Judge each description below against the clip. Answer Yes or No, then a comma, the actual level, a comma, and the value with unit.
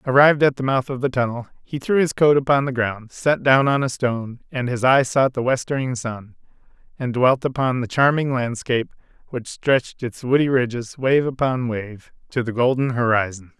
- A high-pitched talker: No, low, 130 Hz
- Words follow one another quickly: No, average, 195 wpm